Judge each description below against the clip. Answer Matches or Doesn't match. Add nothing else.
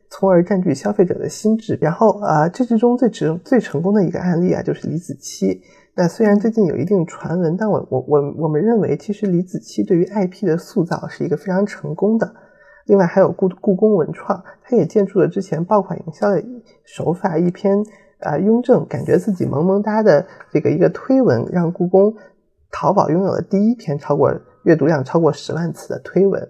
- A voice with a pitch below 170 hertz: Doesn't match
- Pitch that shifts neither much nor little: Matches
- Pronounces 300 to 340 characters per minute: Matches